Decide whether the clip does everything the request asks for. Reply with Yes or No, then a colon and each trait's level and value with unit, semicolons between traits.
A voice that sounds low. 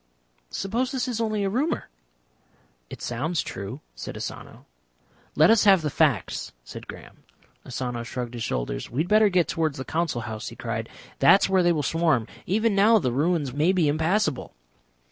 No: medium, 165 Hz